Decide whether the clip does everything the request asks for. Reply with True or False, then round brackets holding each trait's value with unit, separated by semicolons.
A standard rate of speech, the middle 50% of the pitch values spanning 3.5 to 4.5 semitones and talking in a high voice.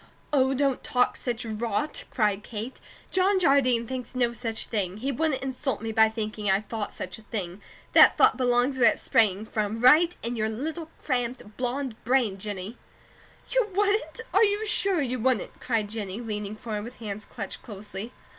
True (175 wpm; 3.8 semitones; 235 Hz)